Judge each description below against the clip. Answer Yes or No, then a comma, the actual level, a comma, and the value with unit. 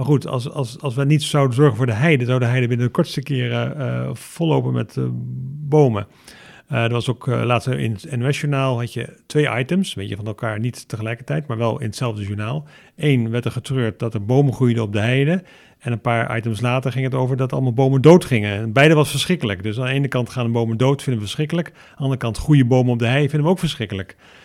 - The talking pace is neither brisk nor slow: No, fast, 245 wpm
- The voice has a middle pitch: No, low, 125 Hz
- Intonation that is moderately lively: Yes, average, 3.6 semitones